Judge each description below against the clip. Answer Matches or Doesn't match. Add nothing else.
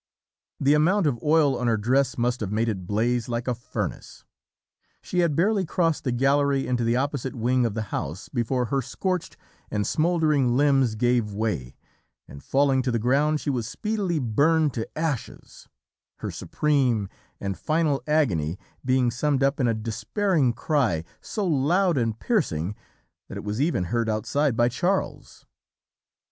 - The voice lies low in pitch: Matches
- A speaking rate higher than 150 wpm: Matches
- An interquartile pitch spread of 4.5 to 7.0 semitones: Matches